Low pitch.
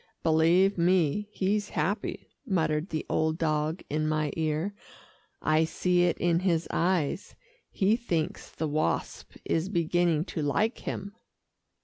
No: medium, 165 Hz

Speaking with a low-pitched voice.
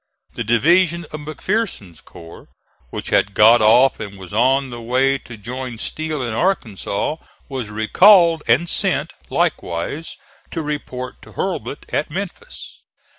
Yes: low, 130 Hz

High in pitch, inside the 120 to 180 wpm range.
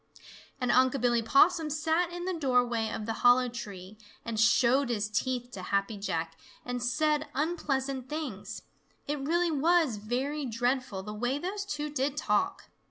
Yes: very high, 255 Hz; average, 160 wpm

